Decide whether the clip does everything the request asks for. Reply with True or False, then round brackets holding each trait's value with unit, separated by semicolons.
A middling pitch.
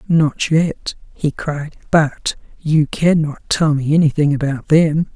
True (155 Hz)